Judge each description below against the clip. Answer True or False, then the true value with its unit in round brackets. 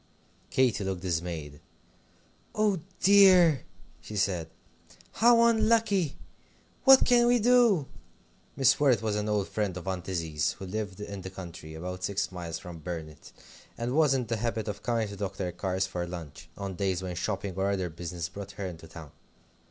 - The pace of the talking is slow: False (165 wpm)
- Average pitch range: False (6.7 semitones)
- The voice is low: True (100 Hz)